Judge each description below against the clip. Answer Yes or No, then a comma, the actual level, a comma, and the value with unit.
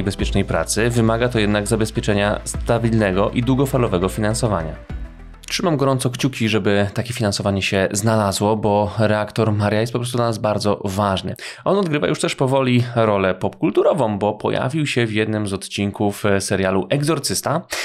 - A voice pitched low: Yes, low, 110 Hz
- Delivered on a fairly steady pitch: No, average, 3.2 semitones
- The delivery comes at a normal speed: Yes, average, 150 wpm